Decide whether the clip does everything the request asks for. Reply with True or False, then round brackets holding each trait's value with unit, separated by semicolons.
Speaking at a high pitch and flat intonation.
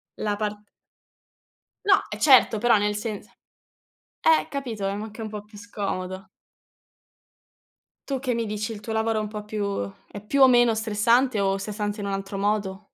True (210 Hz; 2.0 semitones)